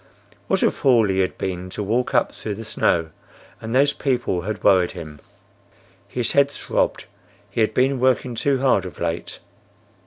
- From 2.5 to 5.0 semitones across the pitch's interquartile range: No, wide, 5.5 semitones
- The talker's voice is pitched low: Yes, low, 110 Hz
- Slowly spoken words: No, average, 175 wpm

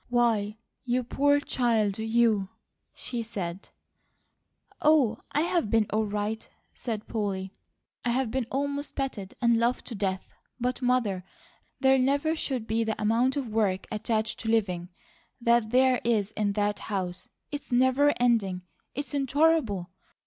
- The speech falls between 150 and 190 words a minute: No, slow, 135 wpm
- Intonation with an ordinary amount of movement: Yes, average, 3.9 semitones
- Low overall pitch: No, high, 230 Hz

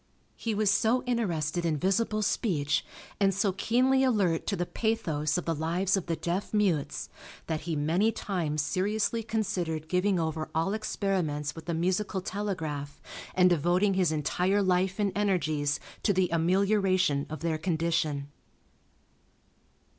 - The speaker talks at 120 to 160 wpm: Yes, average, 145 wpm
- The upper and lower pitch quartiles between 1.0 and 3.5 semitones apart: No, average, 4.2 semitones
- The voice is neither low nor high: Yes, medium, 180 Hz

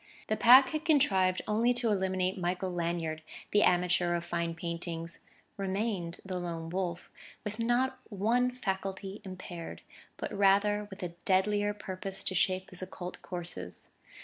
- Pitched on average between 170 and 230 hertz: Yes, high, 190 Hz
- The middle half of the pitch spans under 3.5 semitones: Yes, average, 2.9 semitones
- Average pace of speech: Yes, average, 145 wpm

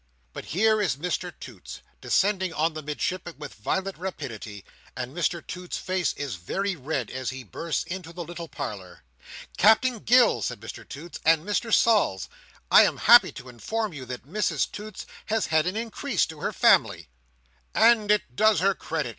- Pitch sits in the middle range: Yes, medium, 170 Hz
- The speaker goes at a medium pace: Yes, average, 170 wpm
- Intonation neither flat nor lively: No, wide, 6.9 semitones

